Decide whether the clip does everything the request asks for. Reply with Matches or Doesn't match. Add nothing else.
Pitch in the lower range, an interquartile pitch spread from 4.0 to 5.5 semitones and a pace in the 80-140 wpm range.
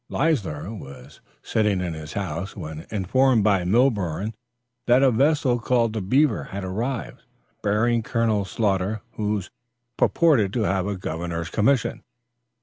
Matches